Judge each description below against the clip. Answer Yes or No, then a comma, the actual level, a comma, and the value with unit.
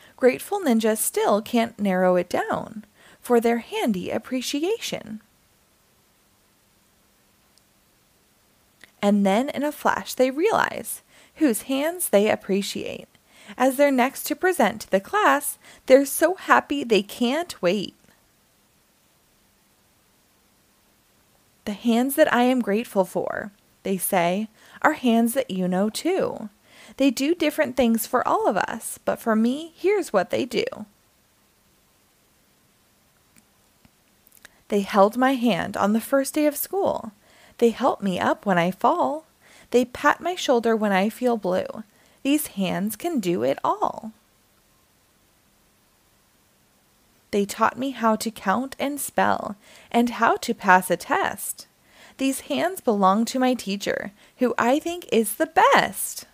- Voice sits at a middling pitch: No, high, 240 Hz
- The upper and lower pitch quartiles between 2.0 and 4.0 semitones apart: No, average, 5.3 semitones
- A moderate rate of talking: No, slow, 130 wpm